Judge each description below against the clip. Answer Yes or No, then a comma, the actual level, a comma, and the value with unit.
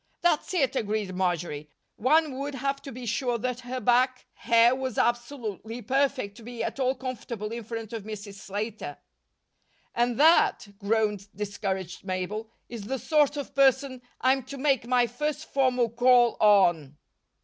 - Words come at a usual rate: Yes, average, 155 wpm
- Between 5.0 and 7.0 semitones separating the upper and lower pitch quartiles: No, average, 4.0 semitones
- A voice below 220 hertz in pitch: No, high, 240 Hz